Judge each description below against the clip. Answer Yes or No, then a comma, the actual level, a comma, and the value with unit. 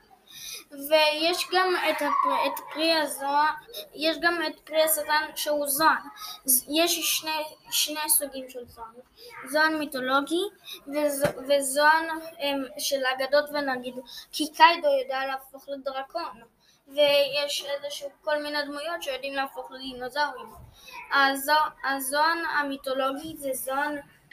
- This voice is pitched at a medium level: No, very high, 295 Hz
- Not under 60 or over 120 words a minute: Yes, slow, 100 wpm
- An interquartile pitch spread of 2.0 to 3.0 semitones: Yes, narrow, 2.4 semitones